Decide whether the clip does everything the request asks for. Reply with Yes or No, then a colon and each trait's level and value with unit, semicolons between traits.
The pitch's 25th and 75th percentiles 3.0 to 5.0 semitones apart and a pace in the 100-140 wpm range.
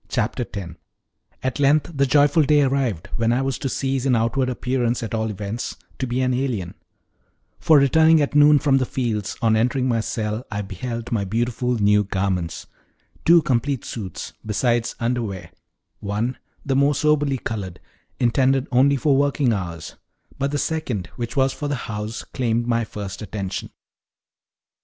No: average, 4.1 semitones; average, 160 wpm